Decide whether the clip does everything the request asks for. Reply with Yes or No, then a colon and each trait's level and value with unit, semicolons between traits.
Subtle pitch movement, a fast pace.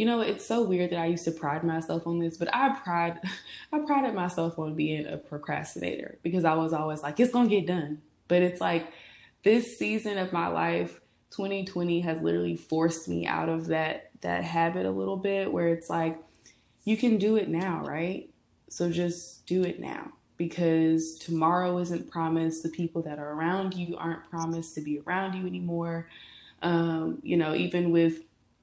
No: narrow, 2.0 semitones; average, 185 wpm